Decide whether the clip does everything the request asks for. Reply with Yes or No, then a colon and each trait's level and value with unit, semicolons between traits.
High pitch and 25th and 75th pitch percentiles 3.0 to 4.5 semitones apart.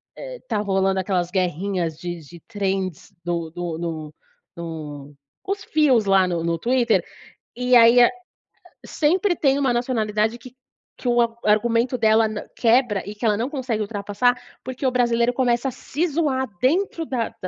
No: high, 225 Hz; average, 5.2 semitones